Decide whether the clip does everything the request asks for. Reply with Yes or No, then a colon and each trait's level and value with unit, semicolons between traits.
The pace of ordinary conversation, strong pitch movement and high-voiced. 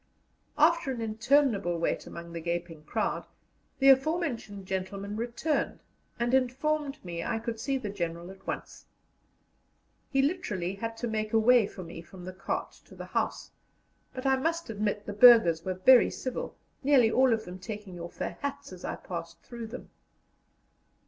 Yes: average, 170 wpm; wide, 5.9 semitones; high, 225 Hz